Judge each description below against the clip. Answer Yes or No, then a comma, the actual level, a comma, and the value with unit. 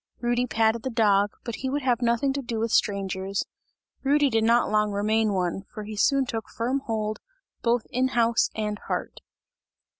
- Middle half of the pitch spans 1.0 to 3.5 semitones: Yes, narrow, 2.6 semitones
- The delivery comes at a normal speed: Yes, average, 180 wpm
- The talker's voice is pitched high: Yes, high, 225 Hz